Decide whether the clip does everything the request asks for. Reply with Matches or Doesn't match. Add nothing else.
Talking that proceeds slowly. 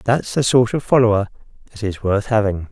Doesn't match